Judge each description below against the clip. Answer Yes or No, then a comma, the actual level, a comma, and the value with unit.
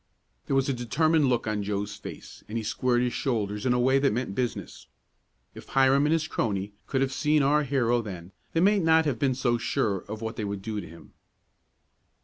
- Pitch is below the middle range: Yes, low, 125 Hz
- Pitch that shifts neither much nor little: Yes, average, 4.5 semitones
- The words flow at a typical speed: No, fast, 215 wpm